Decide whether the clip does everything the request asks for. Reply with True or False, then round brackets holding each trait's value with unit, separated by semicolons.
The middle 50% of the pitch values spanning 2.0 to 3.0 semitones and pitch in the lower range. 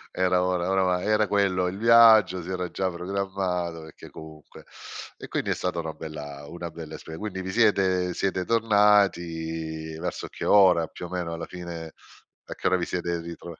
True (2.6 semitones; 90 Hz)